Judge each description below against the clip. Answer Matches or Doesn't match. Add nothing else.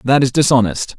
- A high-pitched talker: Doesn't match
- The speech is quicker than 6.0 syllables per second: Doesn't match